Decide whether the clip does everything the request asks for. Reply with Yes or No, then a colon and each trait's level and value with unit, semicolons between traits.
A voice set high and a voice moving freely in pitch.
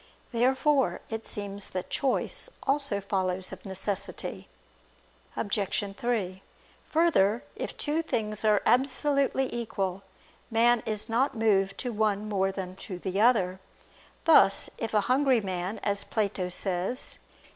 No: high, 210 Hz; average, 4.1 semitones